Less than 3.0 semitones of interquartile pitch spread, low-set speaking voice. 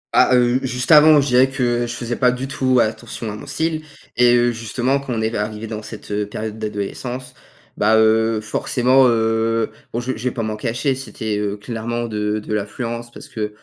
Yes: narrow, 2.5 semitones; low, 115 Hz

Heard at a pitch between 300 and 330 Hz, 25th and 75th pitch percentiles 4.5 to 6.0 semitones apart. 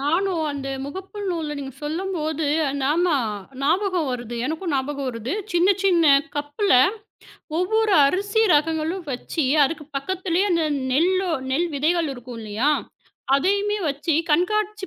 Yes: very high, 325 Hz; average, 4.8 semitones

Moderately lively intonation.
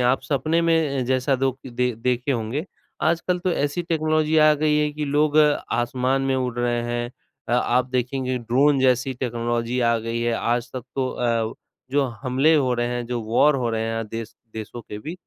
Yes: average, 3.5 semitones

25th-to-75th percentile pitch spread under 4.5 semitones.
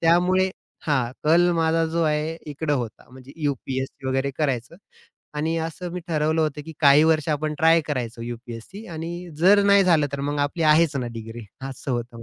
Yes: average, 3.8 semitones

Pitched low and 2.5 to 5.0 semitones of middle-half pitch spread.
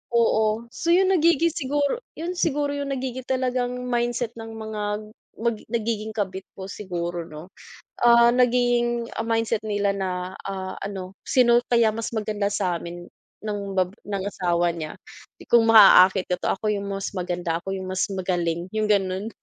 No: high, 215 Hz; average, 4.3 semitones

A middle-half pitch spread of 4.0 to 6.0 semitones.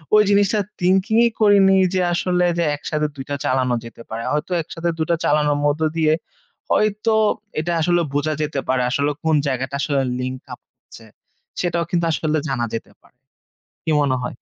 Yes: average, 4.3 semitones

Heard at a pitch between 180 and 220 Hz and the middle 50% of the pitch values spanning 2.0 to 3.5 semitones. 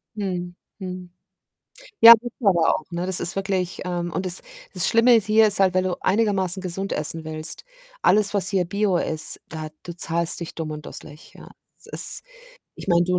Yes: medium, 185 Hz; narrow, 2.6 semitones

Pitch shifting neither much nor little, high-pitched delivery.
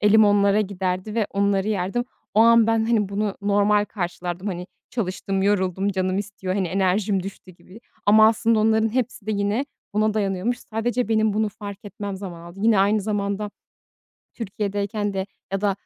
No: narrow, 2.0 semitones; high, 205 Hz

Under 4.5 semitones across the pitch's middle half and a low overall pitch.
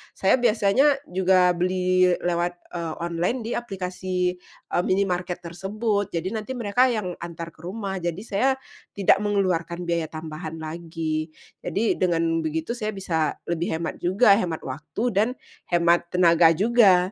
No: average, 3.0 semitones; medium, 180 Hz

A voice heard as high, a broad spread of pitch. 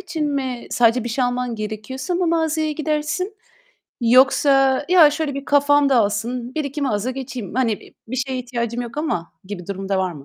No: very high, 260 Hz; average, 4.1 semitones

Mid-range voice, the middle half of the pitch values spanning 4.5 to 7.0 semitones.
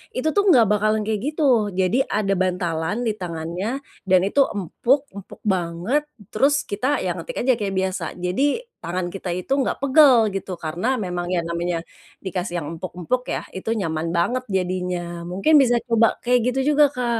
No: high, 195 Hz; wide, 5.6 semitones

